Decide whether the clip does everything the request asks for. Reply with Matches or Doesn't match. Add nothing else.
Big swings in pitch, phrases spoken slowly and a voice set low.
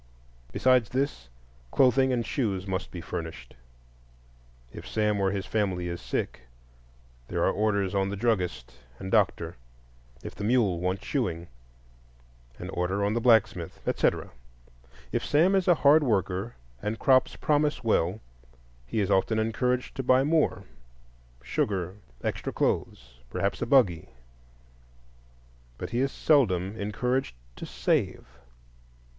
Matches